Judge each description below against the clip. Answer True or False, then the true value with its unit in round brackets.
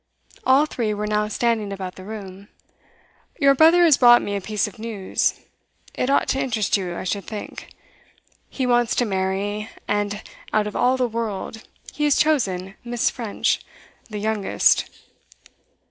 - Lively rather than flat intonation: False (3.4 semitones)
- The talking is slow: False (160 wpm)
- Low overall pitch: False (215 Hz)